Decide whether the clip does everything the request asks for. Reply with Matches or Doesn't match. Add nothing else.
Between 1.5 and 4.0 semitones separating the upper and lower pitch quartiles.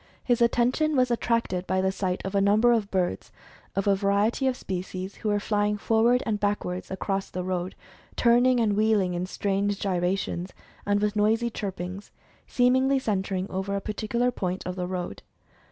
Matches